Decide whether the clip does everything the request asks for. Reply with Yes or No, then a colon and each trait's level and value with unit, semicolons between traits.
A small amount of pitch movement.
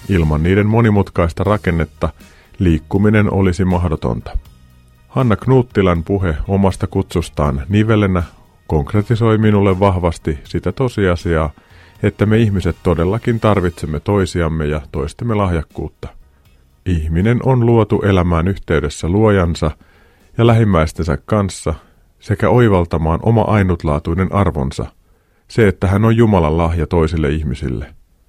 No: average, 4.3 semitones